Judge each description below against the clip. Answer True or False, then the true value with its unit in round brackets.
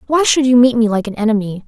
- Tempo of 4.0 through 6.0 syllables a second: False (6.6 syllables/s)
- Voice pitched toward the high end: True (230 Hz)